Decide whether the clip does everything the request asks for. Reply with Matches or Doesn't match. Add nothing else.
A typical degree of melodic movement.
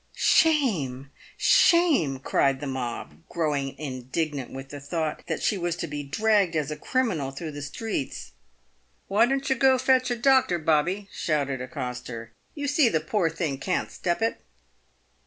Doesn't match